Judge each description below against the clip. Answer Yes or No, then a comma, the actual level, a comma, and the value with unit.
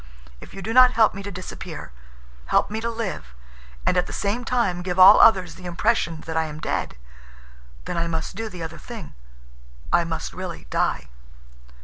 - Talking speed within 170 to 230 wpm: Yes, average, 180 wpm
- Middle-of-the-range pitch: Yes, medium, 175 Hz